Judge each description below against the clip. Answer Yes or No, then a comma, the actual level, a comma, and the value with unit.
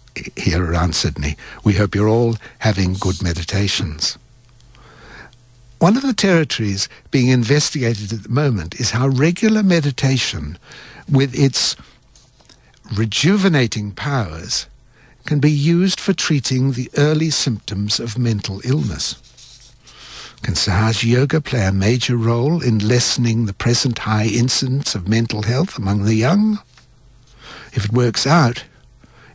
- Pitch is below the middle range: Yes, low, 120 Hz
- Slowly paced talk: Yes, slow, 125 wpm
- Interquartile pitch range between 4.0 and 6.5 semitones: Yes, average, 4.6 semitones